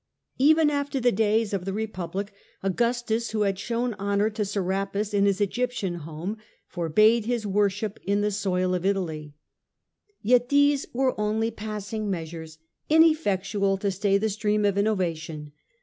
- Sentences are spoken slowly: No, average, 150 wpm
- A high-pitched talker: Yes, high, 205 Hz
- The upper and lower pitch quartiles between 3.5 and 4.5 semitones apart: No, average, 2.8 semitones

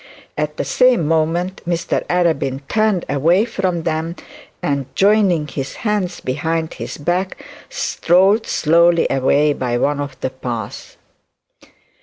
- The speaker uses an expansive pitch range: No, average, 4.3 semitones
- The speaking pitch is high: No, medium, 165 Hz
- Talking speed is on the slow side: Yes, slow, 125 wpm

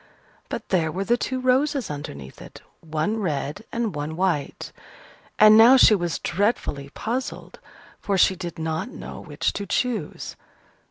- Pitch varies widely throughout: Yes, wide, 6.5 semitones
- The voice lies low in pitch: No, high, 190 Hz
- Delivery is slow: No, average, 150 wpm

